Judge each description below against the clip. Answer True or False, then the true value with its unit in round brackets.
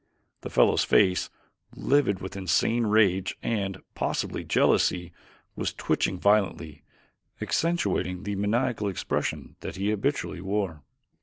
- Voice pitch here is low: True (100 Hz)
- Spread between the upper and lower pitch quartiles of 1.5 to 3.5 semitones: True (2.8 semitones)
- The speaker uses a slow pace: True (110 wpm)